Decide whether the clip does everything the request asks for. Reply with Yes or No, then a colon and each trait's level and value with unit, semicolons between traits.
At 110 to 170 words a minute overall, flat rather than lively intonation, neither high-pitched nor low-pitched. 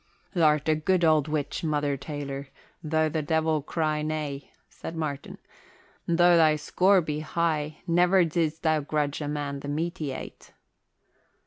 Yes: average, 155 wpm; narrow, 1.9 semitones; medium, 155 Hz